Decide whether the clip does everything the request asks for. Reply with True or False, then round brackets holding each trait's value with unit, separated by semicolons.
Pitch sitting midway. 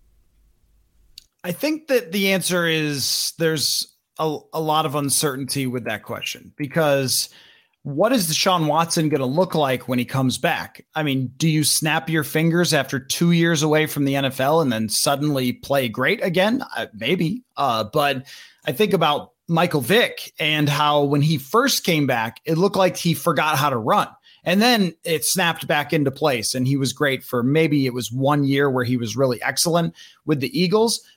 True (150 Hz)